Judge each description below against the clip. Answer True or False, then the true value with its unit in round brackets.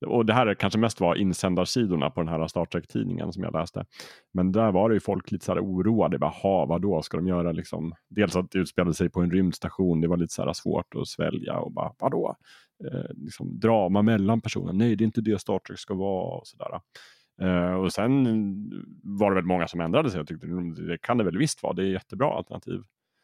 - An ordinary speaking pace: False (225 wpm)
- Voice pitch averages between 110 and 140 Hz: False (95 Hz)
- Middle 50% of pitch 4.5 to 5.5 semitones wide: False (3.6 semitones)